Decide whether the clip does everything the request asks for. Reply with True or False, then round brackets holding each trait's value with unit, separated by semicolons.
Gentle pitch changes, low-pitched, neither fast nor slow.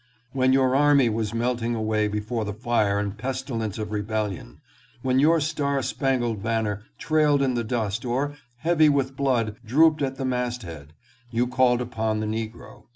False (3.7 semitones; 120 Hz; 165 wpm)